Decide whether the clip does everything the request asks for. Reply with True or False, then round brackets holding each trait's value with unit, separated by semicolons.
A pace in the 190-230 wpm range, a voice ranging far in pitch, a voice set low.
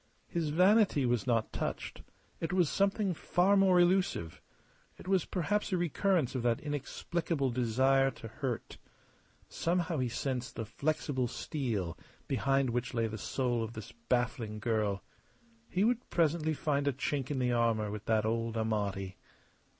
False (150 wpm; 6.7 semitones; 130 Hz)